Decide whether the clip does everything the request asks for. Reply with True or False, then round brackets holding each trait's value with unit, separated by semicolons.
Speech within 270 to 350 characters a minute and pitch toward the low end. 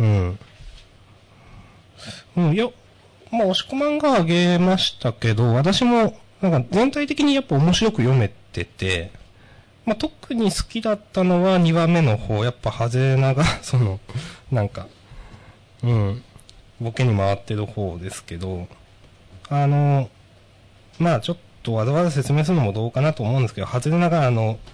True (280 characters per minute; 125 Hz)